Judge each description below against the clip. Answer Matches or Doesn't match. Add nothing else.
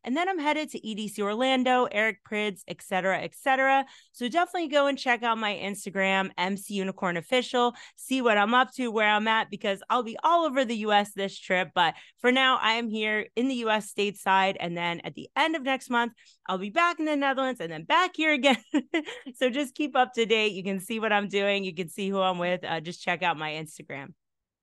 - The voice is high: Matches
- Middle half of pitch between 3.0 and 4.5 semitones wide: Doesn't match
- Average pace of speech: Doesn't match